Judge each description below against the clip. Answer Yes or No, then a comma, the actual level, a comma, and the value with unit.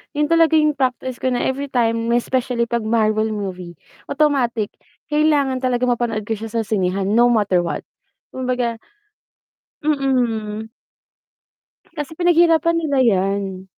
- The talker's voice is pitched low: No, high, 240 Hz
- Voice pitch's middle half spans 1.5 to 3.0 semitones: No, average, 4.3 semitones